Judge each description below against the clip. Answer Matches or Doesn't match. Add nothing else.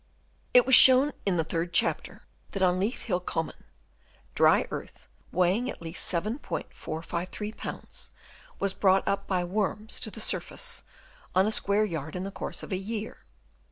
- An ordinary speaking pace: Matches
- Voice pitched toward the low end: Doesn't match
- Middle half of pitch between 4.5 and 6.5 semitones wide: Doesn't match